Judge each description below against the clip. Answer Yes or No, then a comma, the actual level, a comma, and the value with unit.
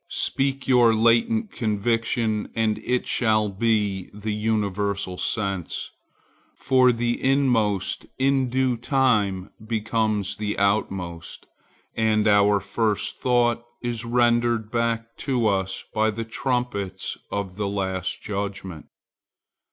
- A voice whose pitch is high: No, low, 110 Hz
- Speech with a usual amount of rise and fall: Yes, average, 3.0 semitones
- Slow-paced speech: Yes, slow, 110 wpm